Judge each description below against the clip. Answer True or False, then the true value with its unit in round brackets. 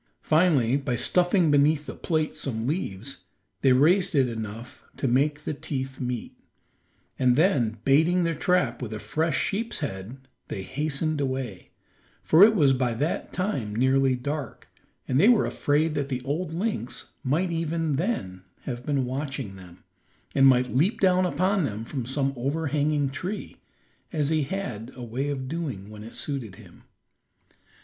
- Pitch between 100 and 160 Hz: True (140 Hz)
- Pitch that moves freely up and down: False (4.4 semitones)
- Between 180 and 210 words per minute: False (160 wpm)